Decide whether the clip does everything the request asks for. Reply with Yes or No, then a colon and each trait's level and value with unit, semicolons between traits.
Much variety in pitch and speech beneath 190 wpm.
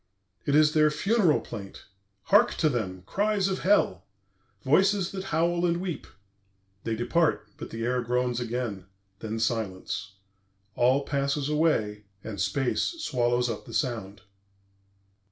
Yes: wide, 7.1 semitones; slow, 135 wpm